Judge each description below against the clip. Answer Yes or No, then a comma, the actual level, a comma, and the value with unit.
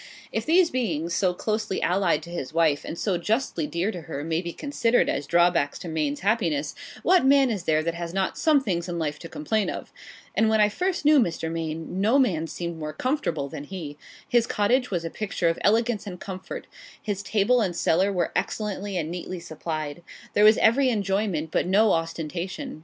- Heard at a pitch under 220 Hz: Yes, medium, 185 Hz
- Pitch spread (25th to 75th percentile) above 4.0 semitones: Yes, average, 5.0 semitones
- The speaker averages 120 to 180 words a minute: No, average, 200 wpm